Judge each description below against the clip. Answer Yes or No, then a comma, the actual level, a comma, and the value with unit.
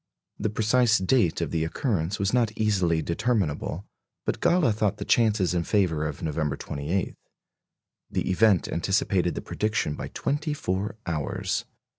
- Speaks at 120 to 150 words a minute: Yes, average, 145 wpm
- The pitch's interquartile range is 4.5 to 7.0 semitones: Yes, average, 4.8 semitones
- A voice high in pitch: No, very low, 95 Hz